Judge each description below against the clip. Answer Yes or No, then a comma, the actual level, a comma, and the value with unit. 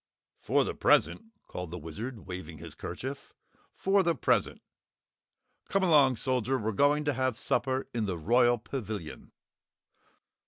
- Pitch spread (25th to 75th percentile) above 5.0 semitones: Yes, wide, 5.5 semitones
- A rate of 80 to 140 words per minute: Yes, slow, 135 wpm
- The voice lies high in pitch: No, low, 125 Hz